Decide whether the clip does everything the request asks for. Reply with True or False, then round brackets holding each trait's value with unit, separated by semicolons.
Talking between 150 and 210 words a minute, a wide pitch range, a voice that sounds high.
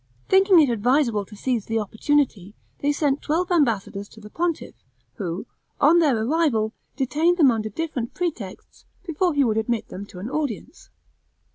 True (160 wpm; 6.3 semitones; 255 Hz)